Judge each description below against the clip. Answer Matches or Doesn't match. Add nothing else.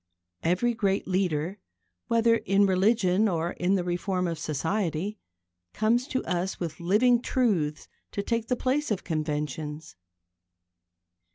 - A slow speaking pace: Matches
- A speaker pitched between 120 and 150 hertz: Doesn't match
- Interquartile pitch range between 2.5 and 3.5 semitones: Doesn't match